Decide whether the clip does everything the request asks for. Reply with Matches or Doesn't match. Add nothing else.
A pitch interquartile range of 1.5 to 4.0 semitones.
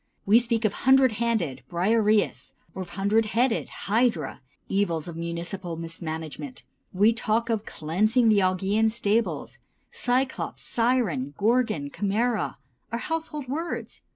Doesn't match